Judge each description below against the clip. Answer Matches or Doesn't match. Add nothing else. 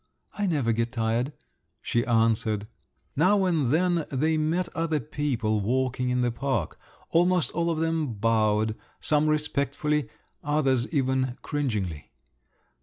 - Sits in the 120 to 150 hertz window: Matches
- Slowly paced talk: Matches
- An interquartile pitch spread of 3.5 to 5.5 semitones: Matches